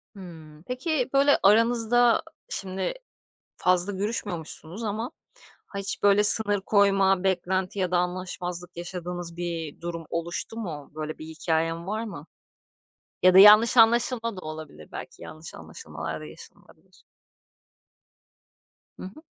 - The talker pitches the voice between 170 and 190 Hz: Yes, medium, 185 Hz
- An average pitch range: Yes, average, 4.0 semitones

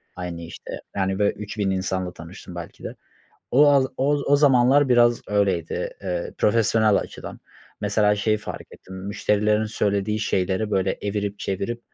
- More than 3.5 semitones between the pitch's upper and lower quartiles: No, average, 2.7 semitones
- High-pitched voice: No, low, 105 Hz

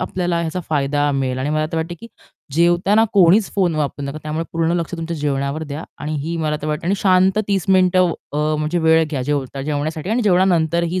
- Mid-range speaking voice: Yes, medium, 160 Hz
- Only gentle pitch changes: No, average, 3.1 semitones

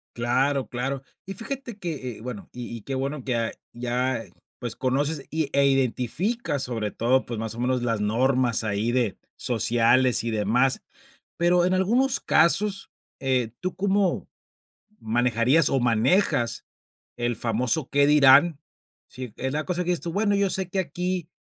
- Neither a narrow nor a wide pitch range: No, wide, 6.2 semitones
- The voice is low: Yes, low, 130 Hz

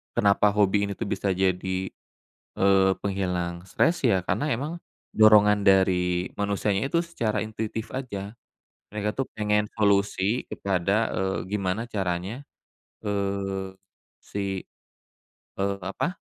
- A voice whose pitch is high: No, low, 100 Hz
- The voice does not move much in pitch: Yes, narrow, 1.8 semitones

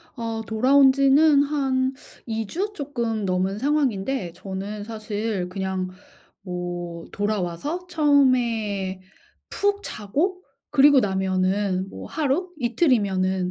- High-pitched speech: Yes, high, 225 Hz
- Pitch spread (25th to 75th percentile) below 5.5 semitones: No, wide, 6.7 semitones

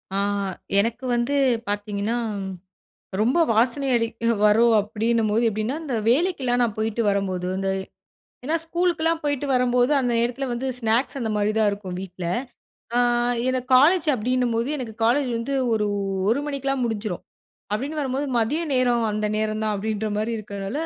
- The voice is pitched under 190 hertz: No, high, 235 Hz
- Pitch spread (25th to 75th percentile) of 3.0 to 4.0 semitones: Yes, average, 3.7 semitones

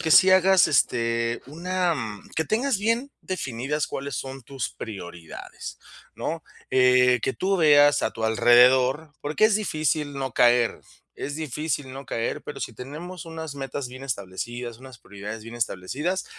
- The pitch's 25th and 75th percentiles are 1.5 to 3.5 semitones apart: No, average, 5.0 semitones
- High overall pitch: No, low, 135 Hz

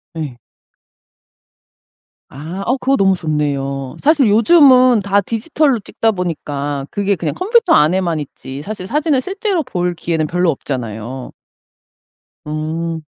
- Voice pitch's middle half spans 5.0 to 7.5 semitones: No, wide, 9.0 semitones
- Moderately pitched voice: Yes, medium, 180 Hz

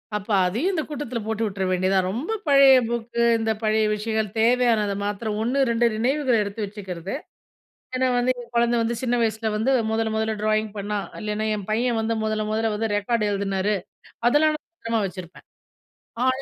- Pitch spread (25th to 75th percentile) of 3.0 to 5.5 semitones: No, narrow, 2.5 semitones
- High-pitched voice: Yes, high, 220 Hz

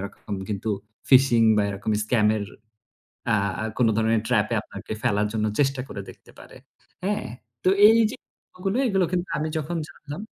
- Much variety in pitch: Yes, wide, 8.2 semitones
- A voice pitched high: No, low, 125 Hz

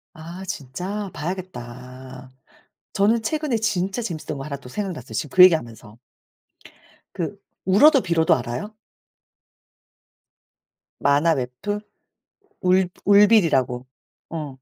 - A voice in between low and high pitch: Yes, medium, 165 Hz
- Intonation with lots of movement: Yes, wide, 7.4 semitones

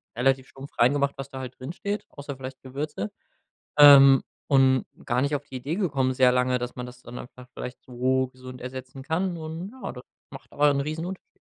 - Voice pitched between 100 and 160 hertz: Yes, low, 135 Hz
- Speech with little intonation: Yes, narrow, 2.3 semitones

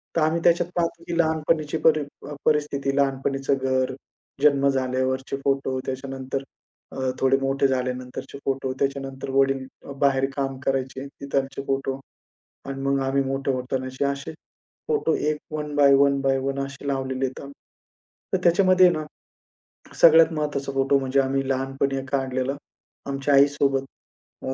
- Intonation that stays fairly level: Yes, narrow, 1.1 semitones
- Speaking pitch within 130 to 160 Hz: Yes, low, 135 Hz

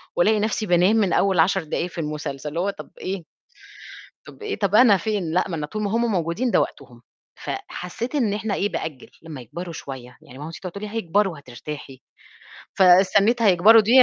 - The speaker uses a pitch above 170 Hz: Yes, medium, 185 Hz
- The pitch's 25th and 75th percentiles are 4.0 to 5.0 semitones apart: Yes, average, 4.7 semitones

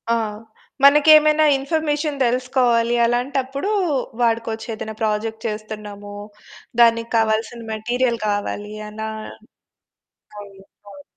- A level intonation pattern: No, average, 3.7 semitones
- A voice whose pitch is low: No, high, 230 Hz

